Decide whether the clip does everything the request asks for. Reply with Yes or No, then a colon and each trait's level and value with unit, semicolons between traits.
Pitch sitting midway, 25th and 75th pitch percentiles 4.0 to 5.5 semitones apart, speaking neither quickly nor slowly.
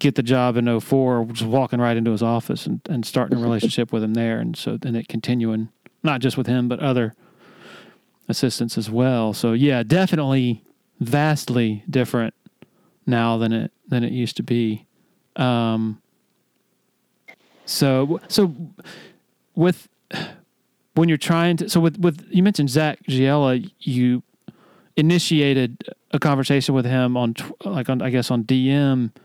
No: low, 130 Hz; average, 4.3 semitones; average, 155 wpm